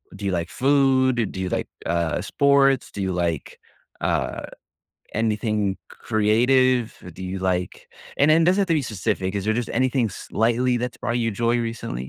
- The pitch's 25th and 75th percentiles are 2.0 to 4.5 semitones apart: No, average, 5.0 semitones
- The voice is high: No, low, 115 Hz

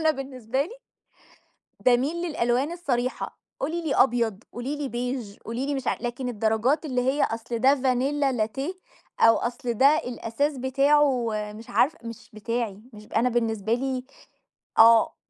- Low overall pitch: No, very high, 250 Hz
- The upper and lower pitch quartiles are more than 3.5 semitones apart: No, average, 3.2 semitones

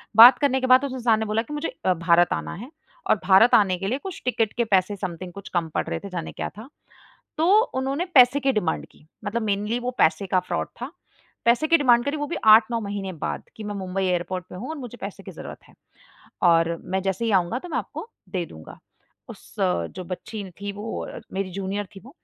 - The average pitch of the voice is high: Yes, high, 210 Hz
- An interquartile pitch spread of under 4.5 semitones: No, average, 5.1 semitones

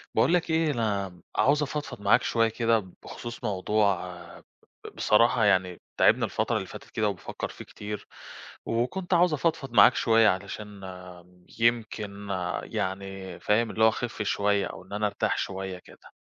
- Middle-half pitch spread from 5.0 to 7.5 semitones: No, average, 3.2 semitones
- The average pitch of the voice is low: Yes, low, 105 Hz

